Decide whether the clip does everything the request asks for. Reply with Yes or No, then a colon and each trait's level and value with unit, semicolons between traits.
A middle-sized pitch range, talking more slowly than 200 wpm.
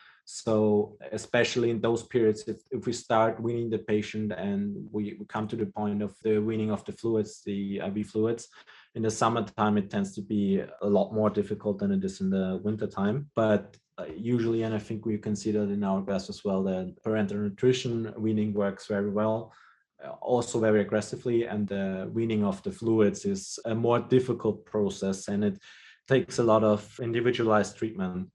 No: narrow, 1.9 semitones; average, 185 wpm